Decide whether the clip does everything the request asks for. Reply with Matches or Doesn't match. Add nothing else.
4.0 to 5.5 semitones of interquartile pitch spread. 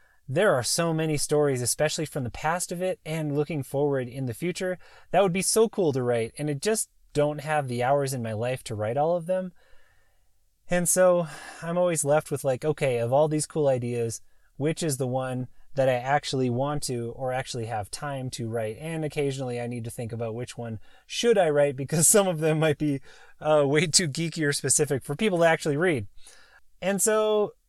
Matches